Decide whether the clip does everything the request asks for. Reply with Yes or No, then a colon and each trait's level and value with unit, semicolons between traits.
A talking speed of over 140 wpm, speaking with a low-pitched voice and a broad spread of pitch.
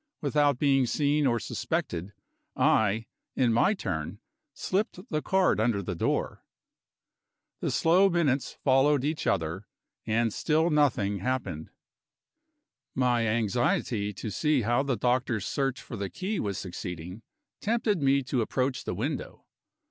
No: slow, 135 wpm; low, 125 Hz; wide, 5.8 semitones